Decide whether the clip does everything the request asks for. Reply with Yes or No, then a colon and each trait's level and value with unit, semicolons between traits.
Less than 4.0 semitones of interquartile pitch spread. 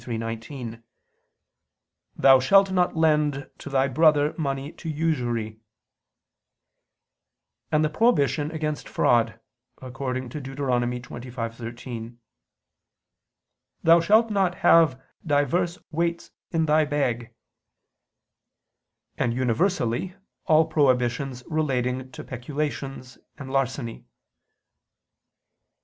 No: average, 4.3 semitones